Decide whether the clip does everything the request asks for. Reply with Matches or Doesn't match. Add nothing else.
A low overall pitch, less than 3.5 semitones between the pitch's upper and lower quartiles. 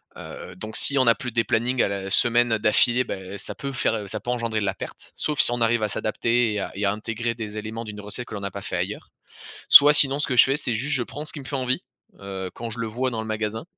Matches